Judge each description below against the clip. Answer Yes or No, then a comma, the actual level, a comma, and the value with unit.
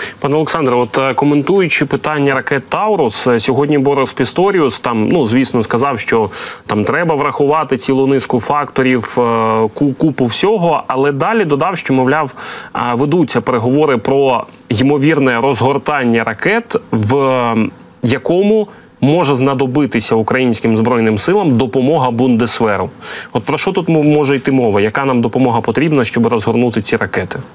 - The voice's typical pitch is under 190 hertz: Yes, low, 135 Hz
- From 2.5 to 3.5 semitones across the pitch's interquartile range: Yes, average, 3.1 semitones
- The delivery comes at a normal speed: Yes, average, 125 wpm